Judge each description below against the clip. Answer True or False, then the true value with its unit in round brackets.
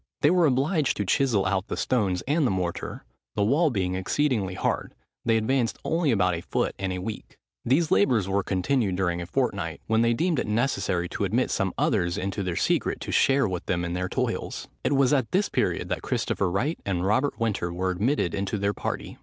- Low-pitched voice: True (105 Hz)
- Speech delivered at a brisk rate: True (210 wpm)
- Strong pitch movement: True (6.3 semitones)